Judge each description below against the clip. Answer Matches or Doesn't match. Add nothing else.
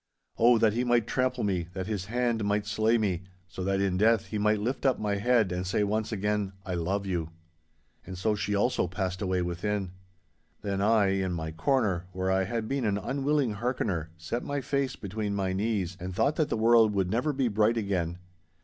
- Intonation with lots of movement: Doesn't match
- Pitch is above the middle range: Doesn't match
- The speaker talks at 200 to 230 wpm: Matches